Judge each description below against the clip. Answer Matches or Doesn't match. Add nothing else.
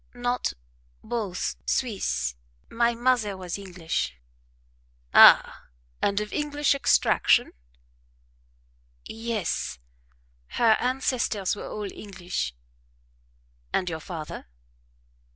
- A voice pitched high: Matches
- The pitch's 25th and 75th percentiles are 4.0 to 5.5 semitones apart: Matches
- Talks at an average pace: Doesn't match